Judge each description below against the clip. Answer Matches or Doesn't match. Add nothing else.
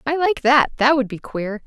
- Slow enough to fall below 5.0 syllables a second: Matches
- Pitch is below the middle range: Doesn't match